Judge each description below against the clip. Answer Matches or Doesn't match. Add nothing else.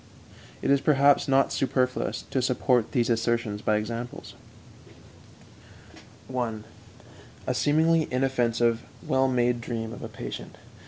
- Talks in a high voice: Doesn't match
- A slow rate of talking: Matches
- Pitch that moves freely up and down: Doesn't match